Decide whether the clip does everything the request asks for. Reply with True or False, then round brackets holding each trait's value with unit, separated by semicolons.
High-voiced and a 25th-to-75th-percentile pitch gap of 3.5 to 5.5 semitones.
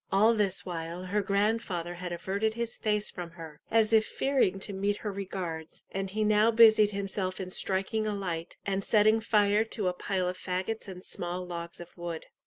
False (195 Hz; 2.9 semitones)